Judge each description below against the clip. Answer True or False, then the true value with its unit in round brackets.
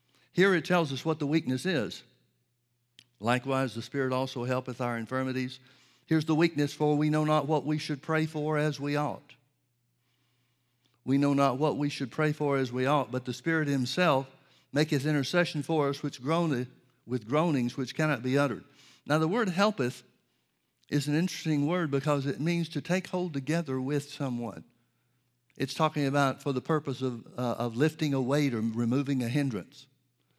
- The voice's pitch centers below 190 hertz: True (140 Hz)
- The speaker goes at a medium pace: True (180 wpm)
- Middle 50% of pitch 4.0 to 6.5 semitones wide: False (3.3 semitones)